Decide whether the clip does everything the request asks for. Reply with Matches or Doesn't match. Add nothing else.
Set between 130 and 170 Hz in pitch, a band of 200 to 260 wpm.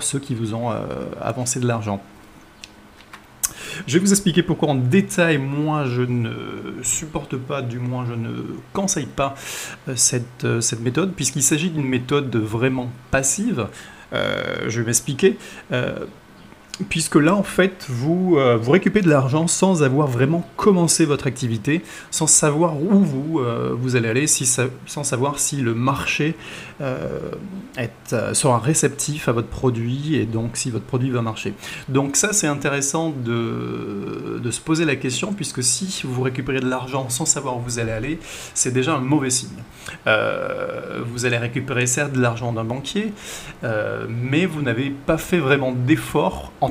Doesn't match